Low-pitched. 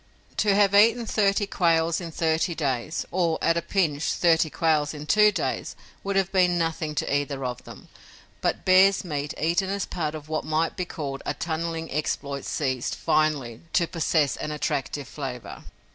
No: medium, 160 Hz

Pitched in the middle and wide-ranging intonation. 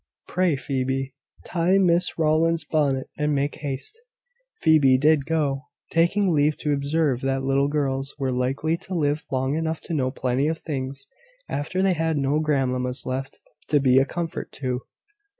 No: medium, 145 Hz; average, 3.2 semitones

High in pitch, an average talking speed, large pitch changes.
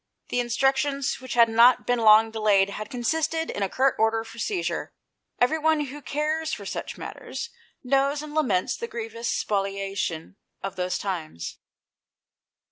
Yes: high, 235 Hz; average, 150 wpm; wide, 5.8 semitones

